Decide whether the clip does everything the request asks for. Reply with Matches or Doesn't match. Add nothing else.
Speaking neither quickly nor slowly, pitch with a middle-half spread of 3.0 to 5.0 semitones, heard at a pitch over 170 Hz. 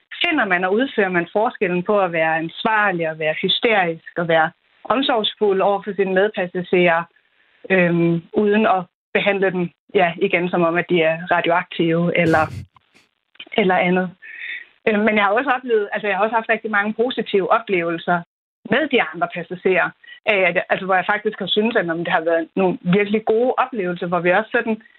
Matches